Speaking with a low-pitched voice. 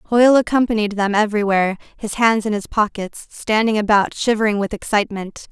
No: high, 215 Hz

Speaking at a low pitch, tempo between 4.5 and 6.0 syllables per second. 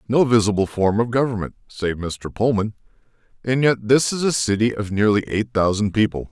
Yes: low, 110 Hz; 5.3 syllables/s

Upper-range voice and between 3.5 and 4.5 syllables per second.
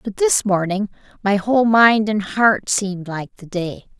Yes: high, 205 Hz; 4.4 syllables/s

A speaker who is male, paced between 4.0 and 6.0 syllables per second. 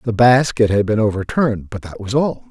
Yes: male; 5.6 syllables/s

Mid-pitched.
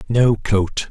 No: low, 110 Hz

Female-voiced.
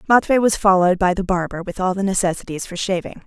Yes: female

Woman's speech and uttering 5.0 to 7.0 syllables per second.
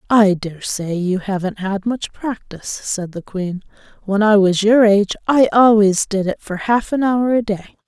No: female; 4.6 syllables/s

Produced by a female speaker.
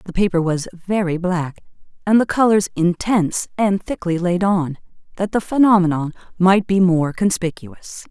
Yes: female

